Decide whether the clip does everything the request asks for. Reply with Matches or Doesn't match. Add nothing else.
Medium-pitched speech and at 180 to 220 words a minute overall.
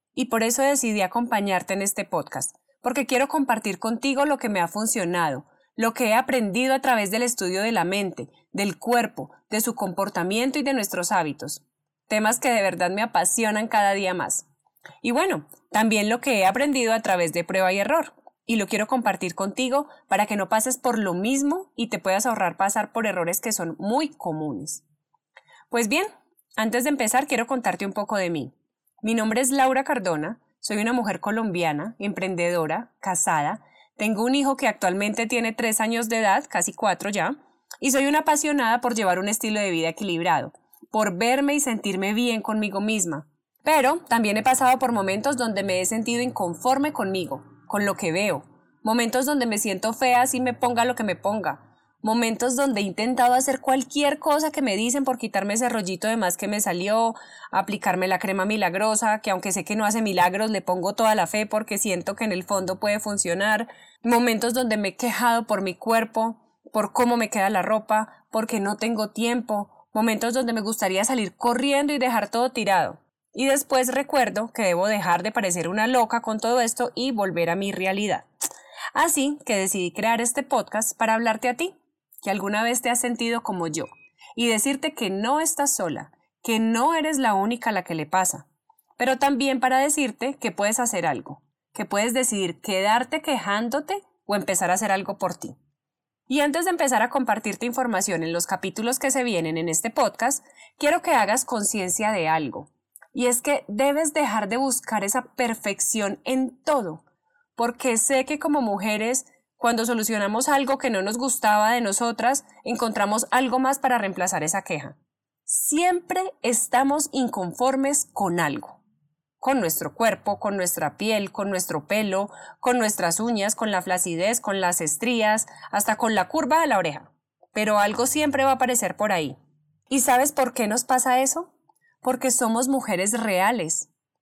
Doesn't match